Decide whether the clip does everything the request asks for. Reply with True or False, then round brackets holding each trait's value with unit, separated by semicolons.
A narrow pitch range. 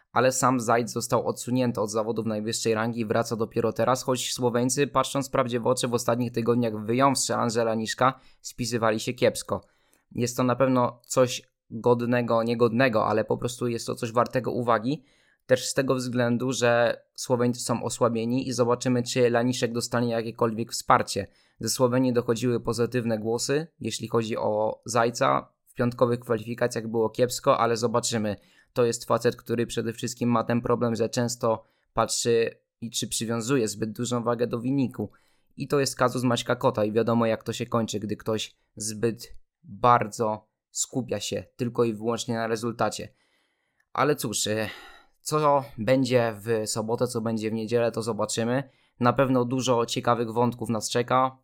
True (1.6 semitones)